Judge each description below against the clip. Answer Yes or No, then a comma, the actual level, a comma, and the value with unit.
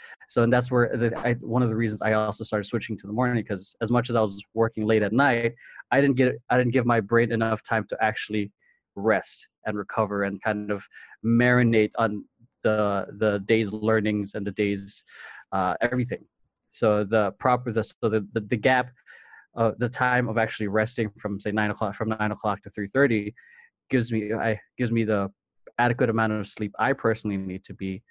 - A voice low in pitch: Yes, low, 110 Hz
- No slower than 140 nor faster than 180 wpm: No, fast, 205 wpm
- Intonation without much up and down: Yes, narrow, 2.3 semitones